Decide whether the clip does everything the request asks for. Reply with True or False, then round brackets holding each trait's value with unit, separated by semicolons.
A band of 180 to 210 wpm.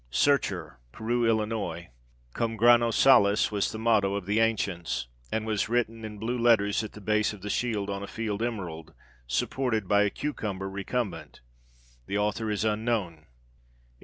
False (160 wpm)